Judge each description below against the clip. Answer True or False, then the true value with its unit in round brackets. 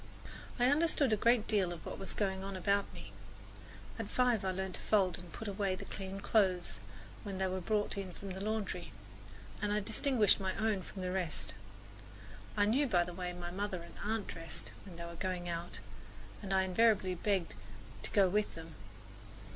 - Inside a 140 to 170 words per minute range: False (195 wpm)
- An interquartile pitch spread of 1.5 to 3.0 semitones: True (2.7 semitones)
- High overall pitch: True (195 Hz)